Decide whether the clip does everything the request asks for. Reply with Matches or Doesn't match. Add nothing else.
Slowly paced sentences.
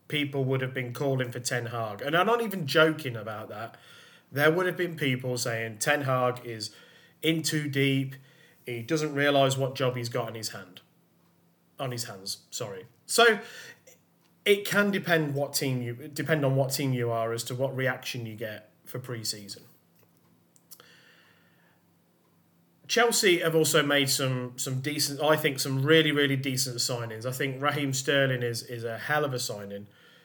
Doesn't match